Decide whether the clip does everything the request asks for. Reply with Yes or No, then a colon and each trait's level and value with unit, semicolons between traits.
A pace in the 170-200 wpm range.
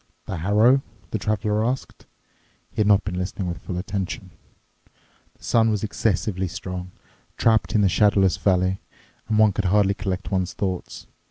No: average, 160 wpm